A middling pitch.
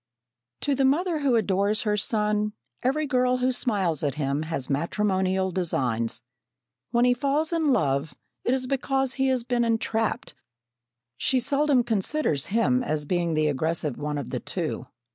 No: high, 220 Hz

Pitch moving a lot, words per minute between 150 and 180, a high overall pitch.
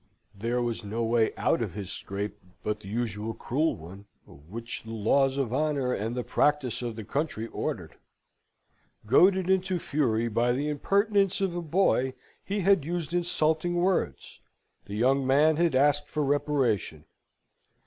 No: wide, 6.0 semitones; average, 155 wpm; low, 130 Hz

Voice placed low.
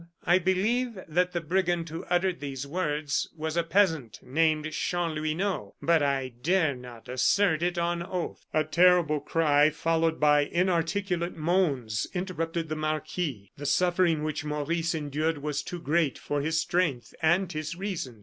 No: medium, 160 Hz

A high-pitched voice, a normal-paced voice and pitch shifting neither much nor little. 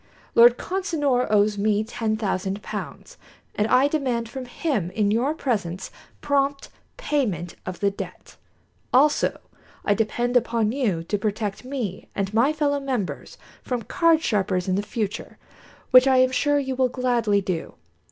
Yes: high, 235 Hz; average, 150 wpm; average, 4.9 semitones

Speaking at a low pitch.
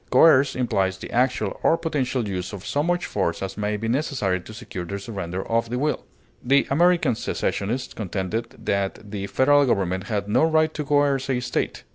Yes: low, 115 Hz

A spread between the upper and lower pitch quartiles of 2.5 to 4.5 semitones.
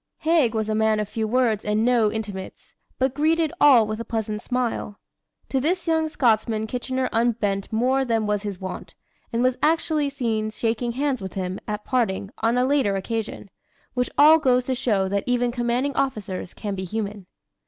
Yes: average, 3.5 semitones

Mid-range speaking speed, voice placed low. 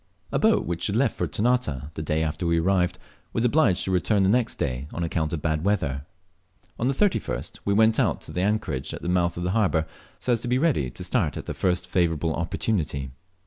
No: fast, 225 wpm; very low, 90 Hz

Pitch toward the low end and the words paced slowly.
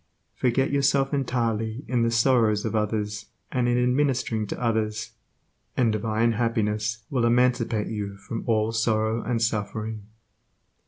Yes: low, 115 Hz; slow, 130 wpm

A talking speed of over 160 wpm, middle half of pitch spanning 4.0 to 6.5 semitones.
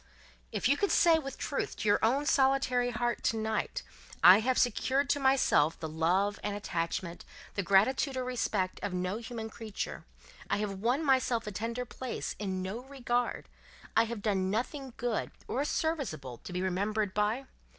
Yes: average, 170 wpm; average, 4.8 semitones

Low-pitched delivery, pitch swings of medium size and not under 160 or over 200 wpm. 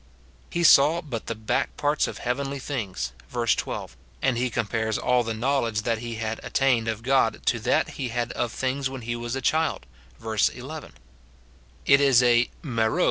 Yes: low, 120 Hz; average, 3.1 semitones; average, 175 wpm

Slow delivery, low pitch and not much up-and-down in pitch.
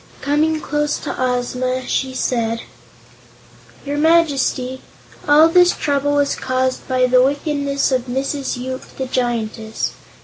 No: slow, 125 wpm; very high, 265 Hz; narrow, 2.3 semitones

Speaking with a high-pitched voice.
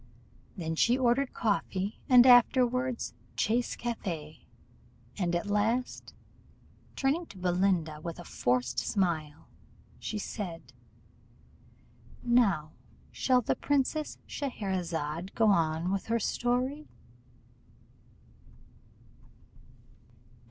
Yes: high, 205 Hz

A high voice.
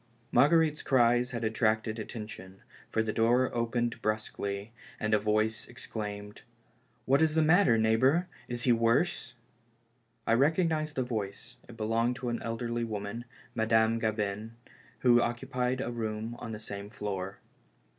No: low, 115 Hz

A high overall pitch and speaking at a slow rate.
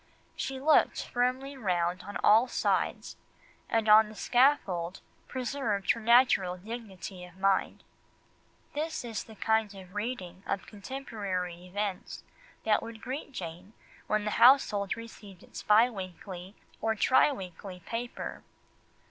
Yes: high, 210 Hz; slow, 130 wpm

